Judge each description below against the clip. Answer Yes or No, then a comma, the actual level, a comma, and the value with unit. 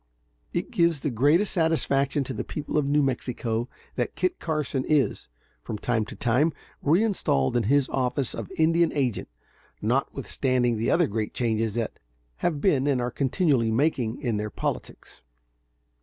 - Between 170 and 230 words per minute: No, average, 155 wpm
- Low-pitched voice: Yes, low, 130 Hz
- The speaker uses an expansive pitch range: No, average, 4.6 semitones